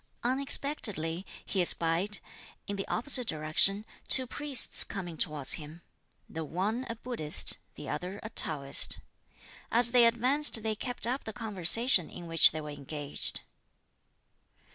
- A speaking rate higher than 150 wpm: No, slow, 135 wpm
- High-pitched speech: Yes, high, 200 Hz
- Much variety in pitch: Yes, wide, 6.8 semitones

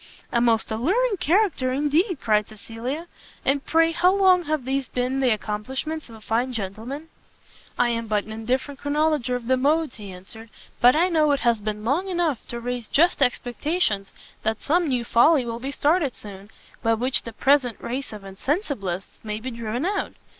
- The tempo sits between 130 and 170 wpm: No, average, 180 wpm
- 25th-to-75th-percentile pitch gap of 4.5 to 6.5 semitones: Yes, wide, 5.5 semitones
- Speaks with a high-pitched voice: Yes, very high, 255 Hz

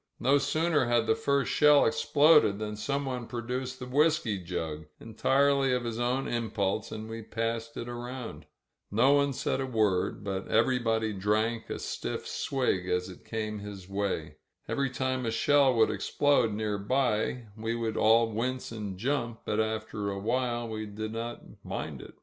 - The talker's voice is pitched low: Yes, low, 115 Hz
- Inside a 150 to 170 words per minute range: Yes, average, 165 wpm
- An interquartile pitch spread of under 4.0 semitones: Yes, average, 3.2 semitones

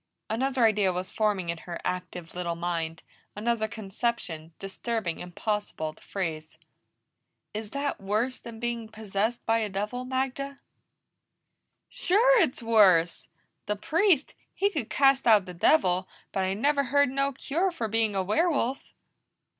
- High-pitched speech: Yes, high, 220 Hz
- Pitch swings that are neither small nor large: No, wide, 5.9 semitones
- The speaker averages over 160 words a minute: No, average, 140 wpm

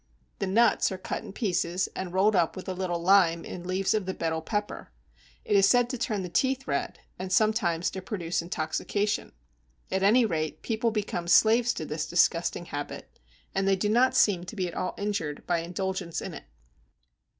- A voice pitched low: No, high, 190 Hz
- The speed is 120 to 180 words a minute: No, average, 195 wpm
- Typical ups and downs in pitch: Yes, average, 3.4 semitones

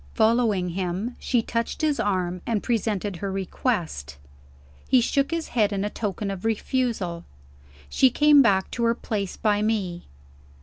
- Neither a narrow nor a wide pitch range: Yes, average, 3.8 semitones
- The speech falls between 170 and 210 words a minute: No, average, 145 wpm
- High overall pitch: Yes, high, 210 Hz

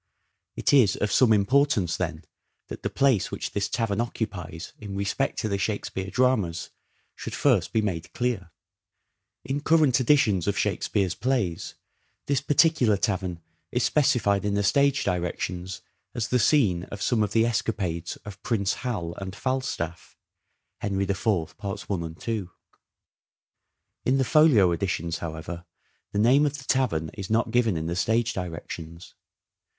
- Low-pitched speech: Yes, low, 100 Hz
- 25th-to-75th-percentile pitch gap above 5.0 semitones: Yes, wide, 5.6 semitones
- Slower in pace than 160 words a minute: Yes, average, 150 wpm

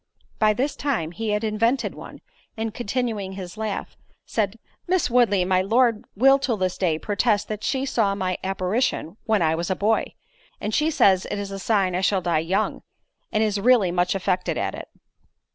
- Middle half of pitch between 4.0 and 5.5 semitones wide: No, average, 3.5 semitones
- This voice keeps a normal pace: Yes, average, 190 wpm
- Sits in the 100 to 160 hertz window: No, high, 205 Hz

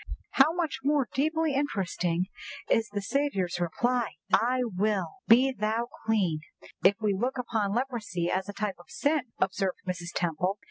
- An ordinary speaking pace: Yes, average, 155 wpm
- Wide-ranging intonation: Yes, wide, 5.9 semitones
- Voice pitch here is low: No, high, 220 Hz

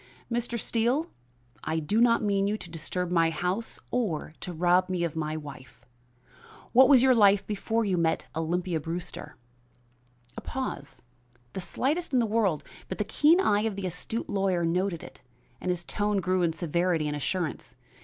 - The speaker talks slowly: No, average, 175 wpm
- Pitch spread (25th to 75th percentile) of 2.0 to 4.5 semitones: No, average, 4.9 semitones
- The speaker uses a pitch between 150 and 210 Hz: Yes, medium, 185 Hz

